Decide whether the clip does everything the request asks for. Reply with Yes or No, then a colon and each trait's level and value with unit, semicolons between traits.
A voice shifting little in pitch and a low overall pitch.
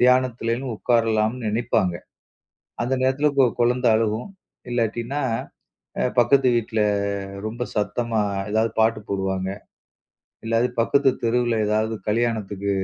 Yes: narrow, 2.2 semitones; low, 115 Hz